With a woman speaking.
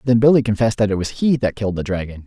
No: male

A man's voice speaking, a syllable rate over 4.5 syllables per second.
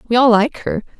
No: female; 5.3 syllables/s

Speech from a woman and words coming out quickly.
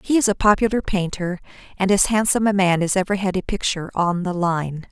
Yes: female; fast, 220 wpm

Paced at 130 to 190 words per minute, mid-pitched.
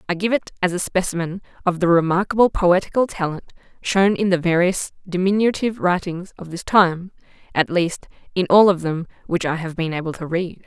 Yes: average, 185 wpm; medium, 180 Hz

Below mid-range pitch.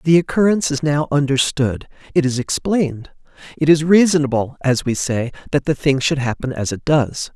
No: medium, 145 Hz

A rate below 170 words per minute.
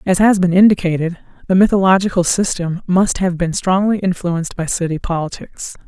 Yes: average, 155 wpm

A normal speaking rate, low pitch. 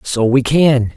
Yes: average, 190 wpm; low, 130 Hz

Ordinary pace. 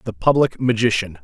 Yes: average, 145 wpm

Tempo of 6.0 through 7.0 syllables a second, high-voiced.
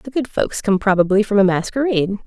Yes: 6.1 syllables/s; high, 210 Hz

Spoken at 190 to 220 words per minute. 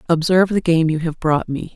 No: fast, 240 wpm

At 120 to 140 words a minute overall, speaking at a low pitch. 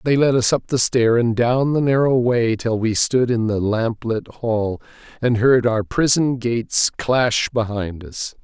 No: average, 190 wpm; low, 120 Hz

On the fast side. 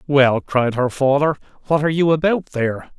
No: average, 180 wpm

